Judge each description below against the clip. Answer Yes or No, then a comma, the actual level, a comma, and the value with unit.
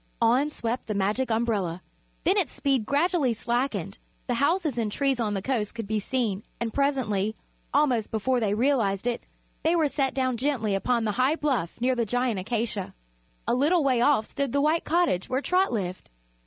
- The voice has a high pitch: Yes, high, 245 Hz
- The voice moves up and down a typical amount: Yes, average, 4.5 semitones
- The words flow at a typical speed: Yes, average, 185 wpm